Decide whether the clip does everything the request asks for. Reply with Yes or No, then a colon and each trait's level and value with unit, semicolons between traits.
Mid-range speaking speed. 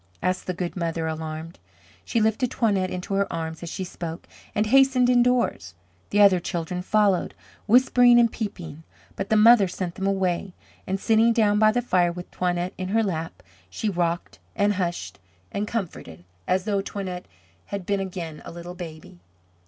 Yes: average, 170 wpm